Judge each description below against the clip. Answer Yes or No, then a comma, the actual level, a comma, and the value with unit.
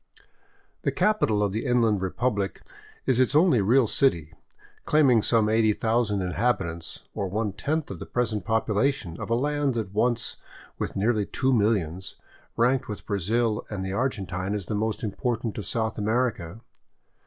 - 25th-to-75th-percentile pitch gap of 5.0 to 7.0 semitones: No, average, 3.5 semitones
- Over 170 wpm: No, average, 155 wpm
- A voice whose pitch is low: Yes, low, 110 Hz